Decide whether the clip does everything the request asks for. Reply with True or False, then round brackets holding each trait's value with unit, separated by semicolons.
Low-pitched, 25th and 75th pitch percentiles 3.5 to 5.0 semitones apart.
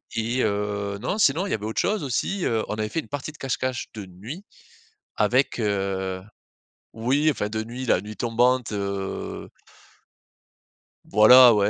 True (110 Hz; 4.1 semitones)